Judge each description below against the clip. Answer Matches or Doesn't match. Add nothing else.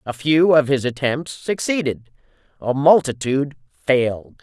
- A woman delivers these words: Doesn't match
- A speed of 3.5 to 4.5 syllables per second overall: Matches